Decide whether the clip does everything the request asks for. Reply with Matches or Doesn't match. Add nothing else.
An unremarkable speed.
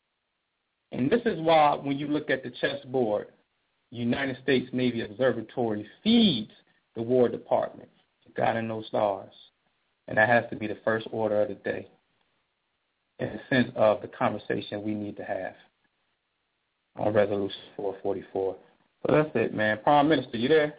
Matches